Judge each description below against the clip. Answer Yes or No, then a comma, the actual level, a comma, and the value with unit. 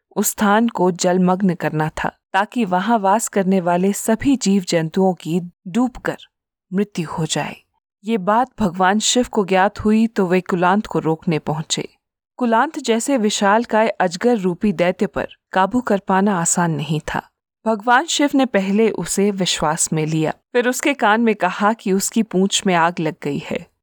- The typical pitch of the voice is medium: No, high, 195 Hz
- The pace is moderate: Yes, average, 165 wpm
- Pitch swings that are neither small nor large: Yes, average, 3.8 semitones